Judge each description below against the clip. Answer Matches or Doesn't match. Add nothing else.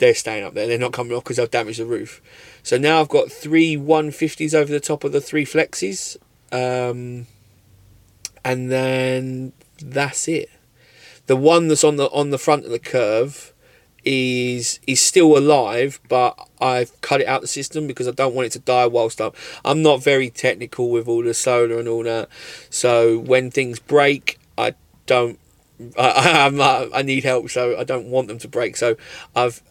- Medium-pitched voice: Doesn't match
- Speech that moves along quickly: Doesn't match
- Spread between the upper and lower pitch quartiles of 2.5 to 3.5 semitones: Matches